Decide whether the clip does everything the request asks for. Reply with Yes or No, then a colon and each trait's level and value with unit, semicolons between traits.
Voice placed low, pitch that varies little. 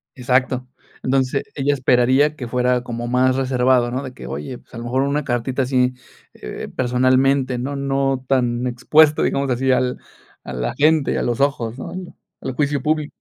Yes: low, 130 Hz; narrow, 1.9 semitones